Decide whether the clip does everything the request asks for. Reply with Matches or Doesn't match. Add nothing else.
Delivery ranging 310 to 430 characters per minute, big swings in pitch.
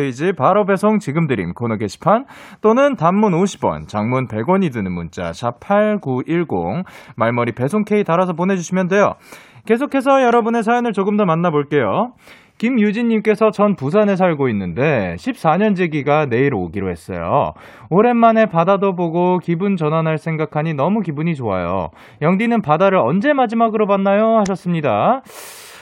Matches